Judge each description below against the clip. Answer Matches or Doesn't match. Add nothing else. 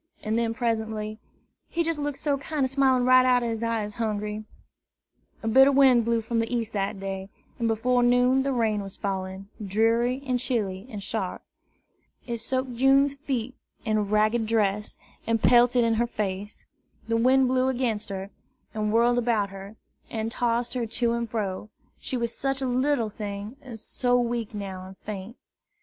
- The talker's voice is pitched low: Doesn't match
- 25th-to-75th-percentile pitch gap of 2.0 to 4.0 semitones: Matches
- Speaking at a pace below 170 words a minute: Doesn't match